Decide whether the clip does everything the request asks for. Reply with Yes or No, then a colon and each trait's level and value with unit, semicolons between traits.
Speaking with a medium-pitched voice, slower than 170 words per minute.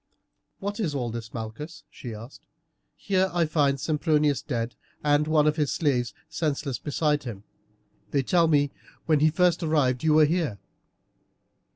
Yes: medium, 150 Hz; average, 155 wpm